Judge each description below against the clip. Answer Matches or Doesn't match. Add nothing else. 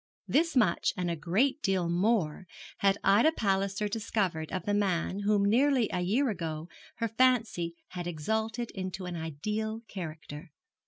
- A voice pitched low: Doesn't match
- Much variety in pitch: Doesn't match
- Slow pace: Doesn't match